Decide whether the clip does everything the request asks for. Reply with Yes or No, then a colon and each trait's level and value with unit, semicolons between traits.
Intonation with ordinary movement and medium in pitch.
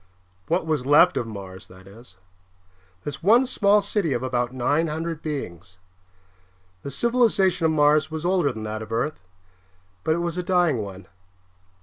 No: wide, 7.1 semitones; medium, 150 Hz